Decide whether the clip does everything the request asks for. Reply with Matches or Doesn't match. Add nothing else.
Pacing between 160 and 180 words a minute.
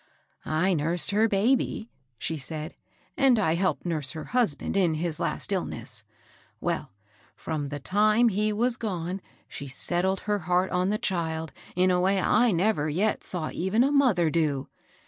Matches